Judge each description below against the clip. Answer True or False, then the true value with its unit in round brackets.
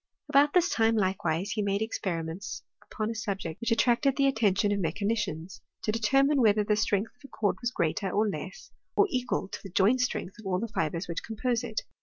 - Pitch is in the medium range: False (215 Hz)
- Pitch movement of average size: True (3.9 semitones)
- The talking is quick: True (210 wpm)